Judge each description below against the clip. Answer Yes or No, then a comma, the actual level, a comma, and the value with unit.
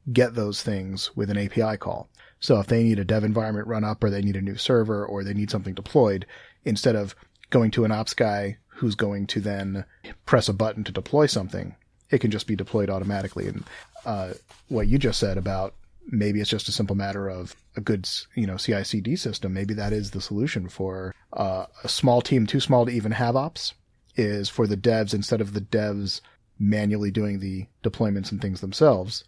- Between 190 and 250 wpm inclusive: Yes, fast, 205 wpm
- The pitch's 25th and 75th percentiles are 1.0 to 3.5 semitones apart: Yes, narrow, 2.5 semitones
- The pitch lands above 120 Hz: No, low, 105 Hz